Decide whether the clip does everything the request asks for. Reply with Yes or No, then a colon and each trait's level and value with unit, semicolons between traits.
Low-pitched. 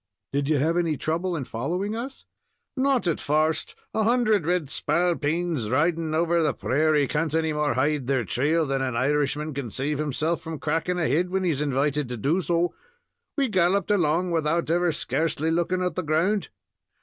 No: medium, 160 Hz